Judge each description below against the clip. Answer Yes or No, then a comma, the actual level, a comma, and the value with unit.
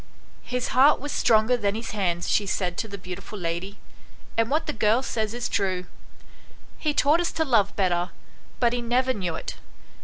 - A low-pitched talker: No, high, 215 Hz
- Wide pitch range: No, average, 4.7 semitones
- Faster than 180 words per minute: Yes, average, 190 wpm